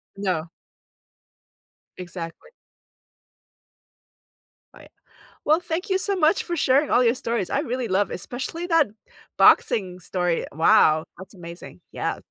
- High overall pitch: Yes, high, 230 Hz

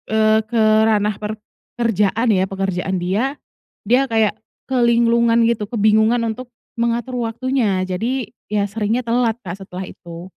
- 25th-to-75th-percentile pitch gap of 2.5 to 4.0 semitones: Yes, average, 2.8 semitones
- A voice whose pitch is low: No, high, 220 Hz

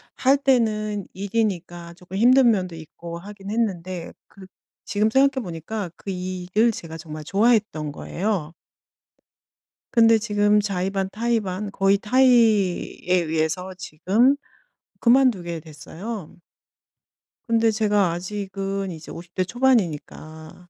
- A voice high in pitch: Yes, high, 195 Hz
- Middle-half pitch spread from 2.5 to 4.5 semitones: Yes, average, 4.2 semitones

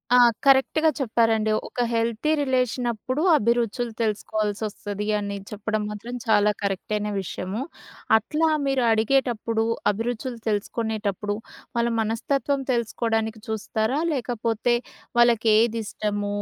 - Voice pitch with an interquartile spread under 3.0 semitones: Yes, narrow, 2.4 semitones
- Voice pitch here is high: Yes, high, 225 Hz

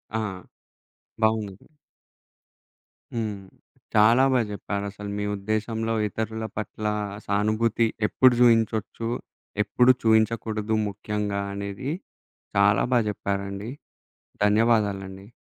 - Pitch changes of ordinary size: No, narrow, 1.9 semitones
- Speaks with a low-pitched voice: Yes, low, 105 Hz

